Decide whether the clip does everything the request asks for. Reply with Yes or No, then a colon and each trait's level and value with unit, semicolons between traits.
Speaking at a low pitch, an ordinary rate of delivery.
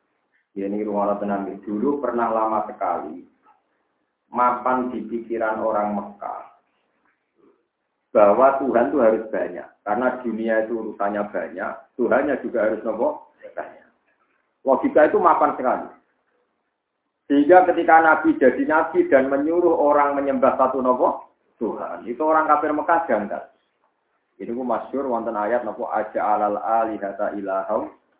Yes: low, 115 Hz; average, 130 wpm